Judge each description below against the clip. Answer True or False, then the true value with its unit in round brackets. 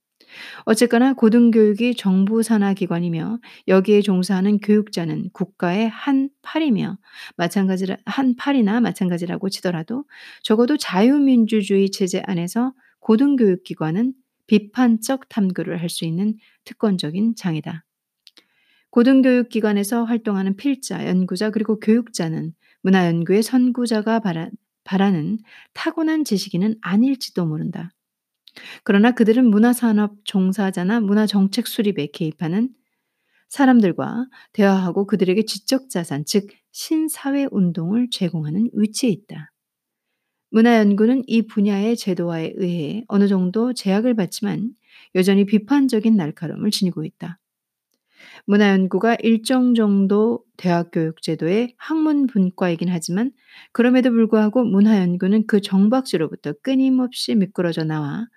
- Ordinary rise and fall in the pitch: True (4.0 semitones)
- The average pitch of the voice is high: True (210 Hz)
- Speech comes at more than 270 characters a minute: True (305 characters per minute)